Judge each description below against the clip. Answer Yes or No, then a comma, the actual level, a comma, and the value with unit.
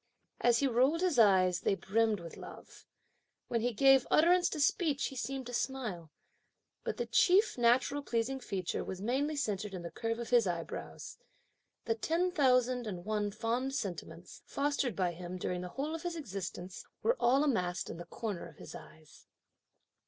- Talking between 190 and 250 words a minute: No, average, 175 wpm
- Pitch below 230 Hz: No, high, 235 Hz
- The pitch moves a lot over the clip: Yes, wide, 6.5 semitones